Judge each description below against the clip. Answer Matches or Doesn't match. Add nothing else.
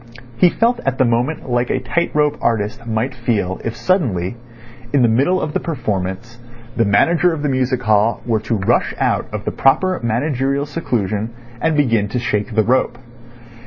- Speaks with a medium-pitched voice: Doesn't match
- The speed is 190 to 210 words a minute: Doesn't match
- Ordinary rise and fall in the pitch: Matches